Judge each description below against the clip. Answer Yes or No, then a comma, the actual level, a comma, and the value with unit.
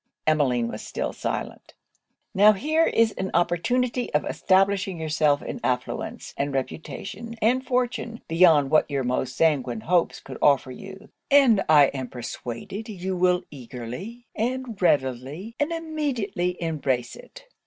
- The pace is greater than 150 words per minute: No, slow, 135 wpm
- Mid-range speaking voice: Yes, medium, 180 Hz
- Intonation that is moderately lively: No, wide, 8.4 semitones